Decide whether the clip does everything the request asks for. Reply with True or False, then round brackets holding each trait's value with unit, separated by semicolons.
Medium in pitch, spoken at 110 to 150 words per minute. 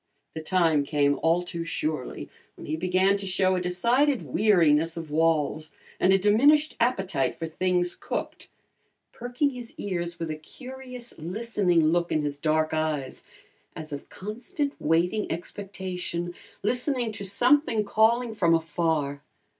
True (180 Hz; 140 wpm)